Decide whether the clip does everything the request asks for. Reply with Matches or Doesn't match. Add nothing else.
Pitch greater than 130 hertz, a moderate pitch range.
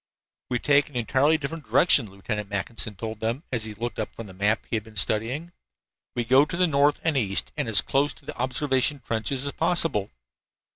Doesn't match